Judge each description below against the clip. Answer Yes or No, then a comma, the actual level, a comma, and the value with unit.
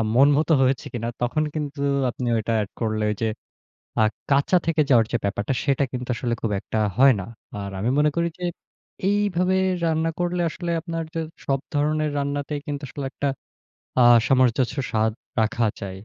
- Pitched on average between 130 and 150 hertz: Yes, medium, 140 Hz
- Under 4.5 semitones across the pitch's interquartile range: No, average, 4.9 semitones